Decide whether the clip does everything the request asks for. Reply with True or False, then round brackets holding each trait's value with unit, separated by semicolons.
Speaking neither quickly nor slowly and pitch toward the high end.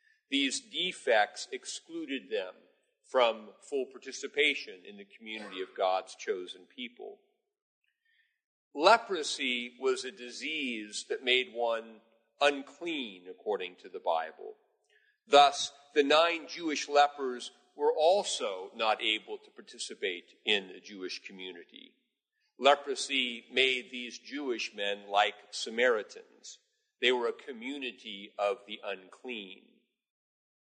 False (110 wpm; 225 Hz)